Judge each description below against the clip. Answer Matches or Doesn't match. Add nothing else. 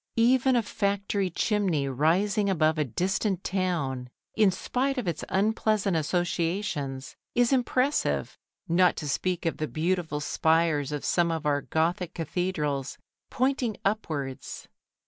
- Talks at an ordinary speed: Doesn't match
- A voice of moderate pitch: Matches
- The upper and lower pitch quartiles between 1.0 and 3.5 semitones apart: Doesn't match